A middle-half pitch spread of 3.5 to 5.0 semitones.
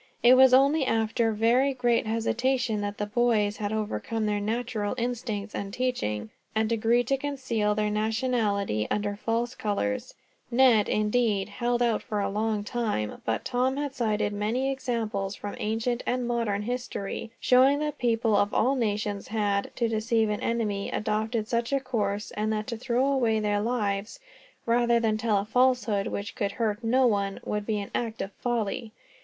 No: average, 2.8 semitones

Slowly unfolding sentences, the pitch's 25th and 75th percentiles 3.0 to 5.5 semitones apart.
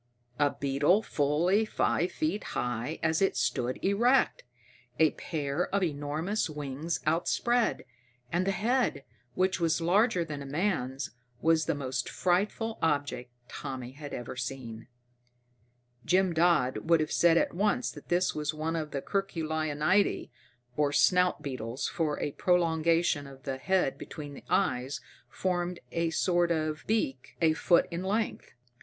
No: average, 145 wpm; average, 4.2 semitones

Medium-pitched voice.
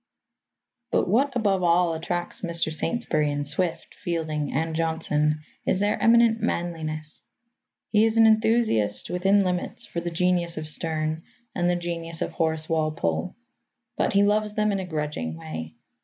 Yes: medium, 170 Hz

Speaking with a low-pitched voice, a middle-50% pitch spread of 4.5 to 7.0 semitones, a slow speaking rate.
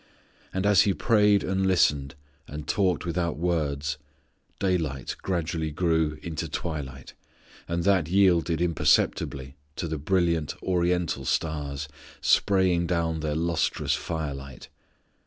No: very low, 85 Hz; average, 3.3 semitones; slow, 120 wpm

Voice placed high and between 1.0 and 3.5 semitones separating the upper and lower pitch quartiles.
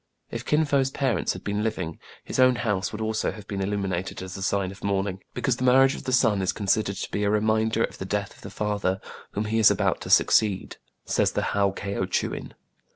No: low, 105 Hz; narrow, 2.5 semitones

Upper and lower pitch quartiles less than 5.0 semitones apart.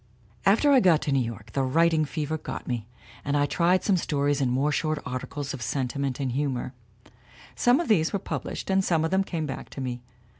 Yes: average, 4.4 semitones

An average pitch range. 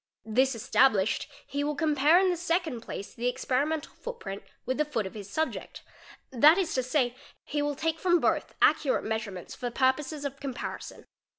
Yes: average, 4.4 semitones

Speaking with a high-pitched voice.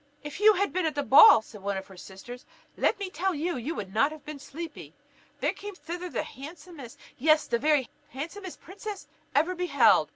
Yes: very high, 305 Hz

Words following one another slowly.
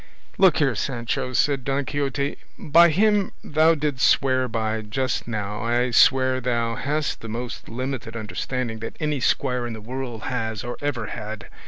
No: average, 165 wpm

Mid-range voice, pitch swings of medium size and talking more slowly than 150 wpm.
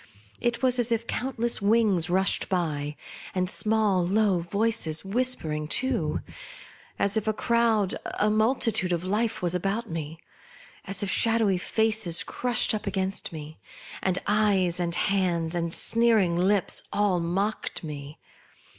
No: high, 195 Hz; average, 4.3 semitones; average, 140 wpm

